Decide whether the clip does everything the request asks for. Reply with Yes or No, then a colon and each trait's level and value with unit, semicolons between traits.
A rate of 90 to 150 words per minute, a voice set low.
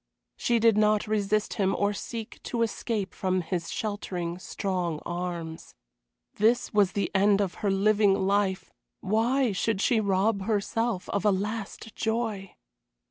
No: average, 140 wpm; high, 205 Hz